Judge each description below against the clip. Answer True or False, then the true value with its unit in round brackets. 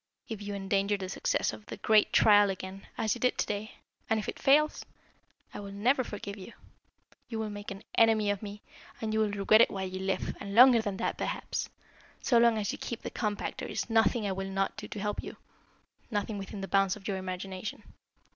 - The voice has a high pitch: True (205 Hz)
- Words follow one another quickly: True (220 wpm)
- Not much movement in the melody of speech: True (2.1 semitones)